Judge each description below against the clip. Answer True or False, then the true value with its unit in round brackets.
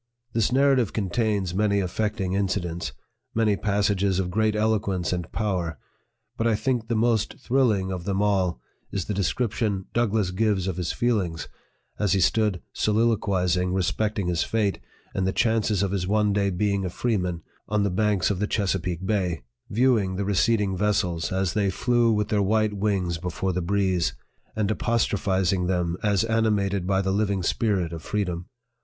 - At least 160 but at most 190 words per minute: True (175 wpm)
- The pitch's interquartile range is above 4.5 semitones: False (2.8 semitones)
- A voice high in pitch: False (100 Hz)